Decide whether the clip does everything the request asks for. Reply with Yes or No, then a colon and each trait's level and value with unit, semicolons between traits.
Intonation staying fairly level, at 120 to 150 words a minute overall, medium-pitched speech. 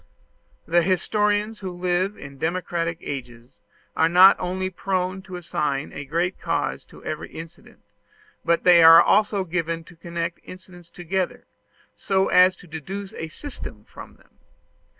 Yes: narrow, 2.3 semitones; average, 145 wpm; medium, 175 Hz